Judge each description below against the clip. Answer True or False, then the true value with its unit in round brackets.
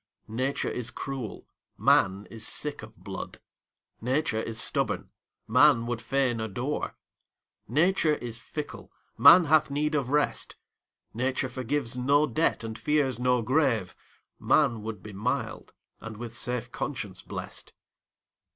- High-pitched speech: False (125 Hz)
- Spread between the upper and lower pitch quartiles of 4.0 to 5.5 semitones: True (4.4 semitones)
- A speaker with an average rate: False (130 wpm)